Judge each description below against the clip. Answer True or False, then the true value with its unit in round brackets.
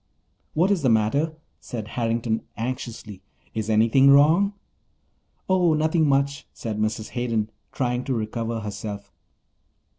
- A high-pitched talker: False (120 Hz)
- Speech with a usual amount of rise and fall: True (4.5 semitones)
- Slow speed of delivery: True (120 wpm)